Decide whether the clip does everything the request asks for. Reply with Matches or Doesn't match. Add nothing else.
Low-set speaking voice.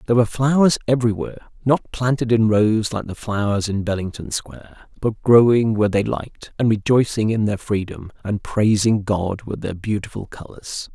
Matches